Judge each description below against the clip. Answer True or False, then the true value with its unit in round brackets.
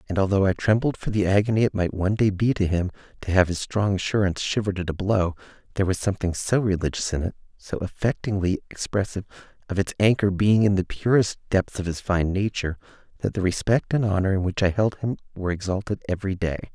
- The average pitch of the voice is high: False (100 Hz)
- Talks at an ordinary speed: False (210 wpm)